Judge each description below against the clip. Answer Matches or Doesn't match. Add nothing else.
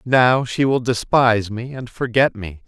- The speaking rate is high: Doesn't match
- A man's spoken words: Matches